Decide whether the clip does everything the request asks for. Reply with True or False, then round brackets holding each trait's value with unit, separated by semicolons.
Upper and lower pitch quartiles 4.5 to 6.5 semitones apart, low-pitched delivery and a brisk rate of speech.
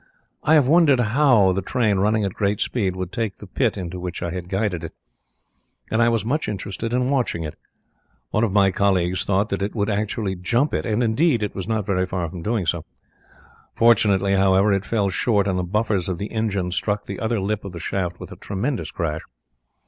False (3.4 semitones; 100 Hz; 215 wpm)